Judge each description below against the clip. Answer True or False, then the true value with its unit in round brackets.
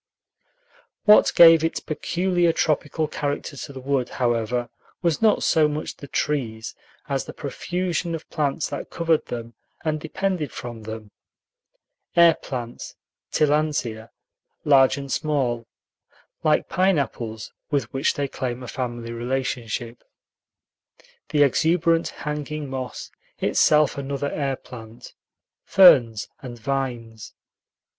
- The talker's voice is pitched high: False (140 Hz)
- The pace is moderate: False (115 wpm)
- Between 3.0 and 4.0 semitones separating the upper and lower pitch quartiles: False (4.4 semitones)